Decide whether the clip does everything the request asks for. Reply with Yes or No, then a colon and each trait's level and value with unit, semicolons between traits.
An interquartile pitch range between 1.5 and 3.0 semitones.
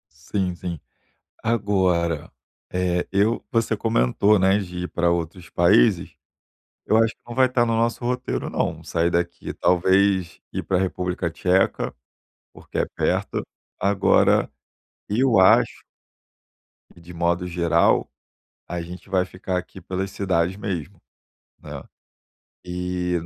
Yes: narrow, 2.6 semitones